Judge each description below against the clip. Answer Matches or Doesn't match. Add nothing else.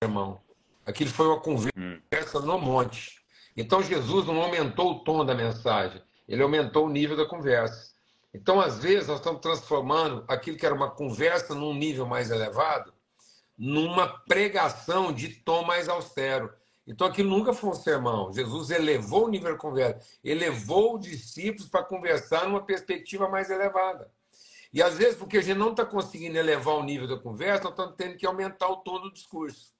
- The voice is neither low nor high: Matches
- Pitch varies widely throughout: Matches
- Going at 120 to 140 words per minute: Doesn't match